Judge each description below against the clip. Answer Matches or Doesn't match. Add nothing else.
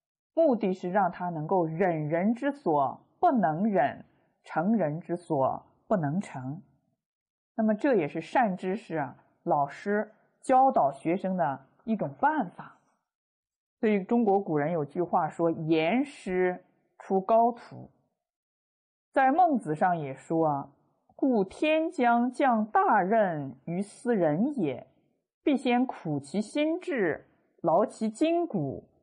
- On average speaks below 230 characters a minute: Matches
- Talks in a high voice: Matches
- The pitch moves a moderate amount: Doesn't match